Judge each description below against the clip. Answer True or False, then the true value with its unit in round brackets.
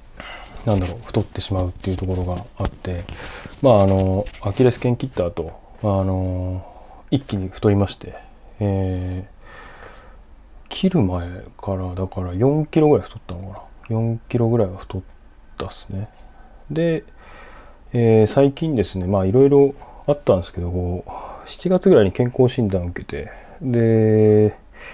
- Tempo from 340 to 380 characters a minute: False (280 characters per minute)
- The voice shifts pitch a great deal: False (4.5 semitones)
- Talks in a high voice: False (100 Hz)